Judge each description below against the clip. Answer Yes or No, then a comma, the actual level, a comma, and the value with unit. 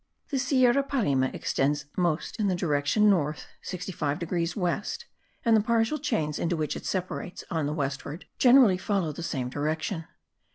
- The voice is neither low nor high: Yes, medium, 175 Hz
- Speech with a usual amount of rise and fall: No, wide, 6.2 semitones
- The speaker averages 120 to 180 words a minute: Yes, average, 160 wpm